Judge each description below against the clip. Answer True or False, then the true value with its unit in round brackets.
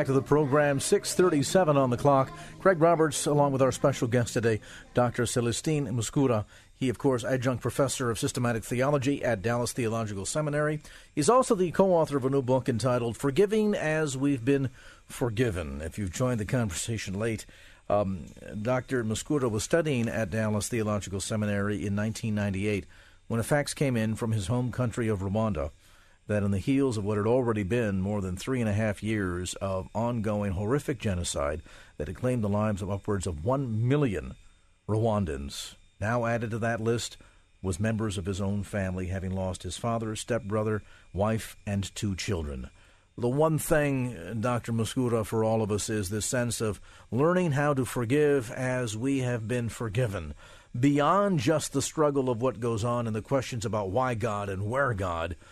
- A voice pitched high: False (115 Hz)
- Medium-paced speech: True (175 wpm)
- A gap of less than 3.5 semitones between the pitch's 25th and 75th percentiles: False (4.6 semitones)